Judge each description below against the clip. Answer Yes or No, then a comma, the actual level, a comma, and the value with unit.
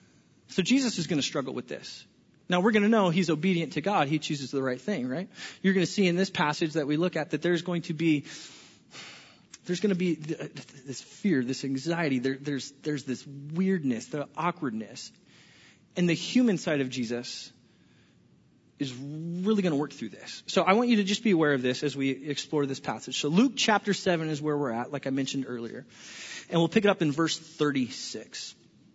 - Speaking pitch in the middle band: Yes, medium, 160 Hz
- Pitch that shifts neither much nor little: Yes, average, 4.9 semitones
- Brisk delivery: Yes, fast, 210 wpm